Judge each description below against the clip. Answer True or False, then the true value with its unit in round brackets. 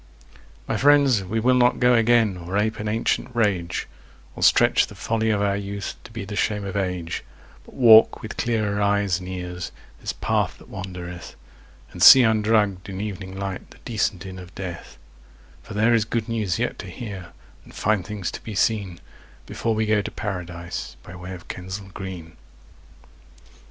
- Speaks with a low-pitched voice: True (100 Hz)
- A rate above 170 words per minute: True (180 wpm)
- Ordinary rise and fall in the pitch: True (3.2 semitones)